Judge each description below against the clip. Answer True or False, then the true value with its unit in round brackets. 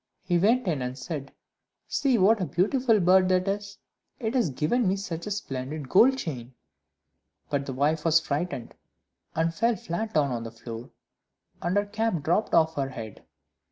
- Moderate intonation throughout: False (6.6 semitones)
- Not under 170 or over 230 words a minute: True (175 wpm)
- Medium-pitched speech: True (170 Hz)